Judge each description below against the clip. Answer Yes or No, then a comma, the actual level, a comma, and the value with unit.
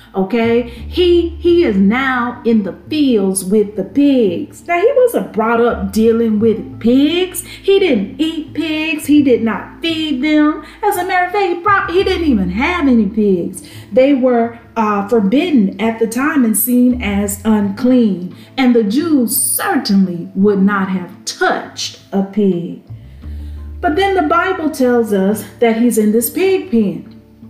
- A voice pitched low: No, high, 235 Hz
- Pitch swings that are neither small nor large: No, wide, 6.9 semitones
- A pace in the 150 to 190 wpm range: Yes, average, 160 wpm